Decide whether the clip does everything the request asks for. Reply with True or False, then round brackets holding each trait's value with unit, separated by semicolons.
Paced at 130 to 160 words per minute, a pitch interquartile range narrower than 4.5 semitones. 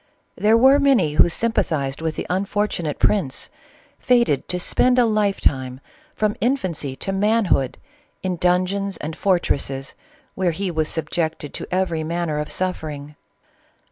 False (145 wpm; 5.2 semitones)